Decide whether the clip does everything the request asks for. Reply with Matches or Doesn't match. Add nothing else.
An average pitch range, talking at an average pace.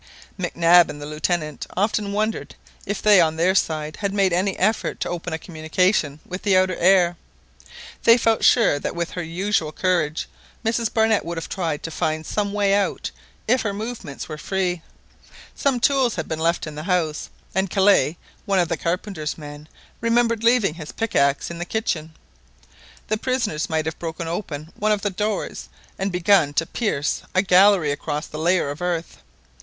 Matches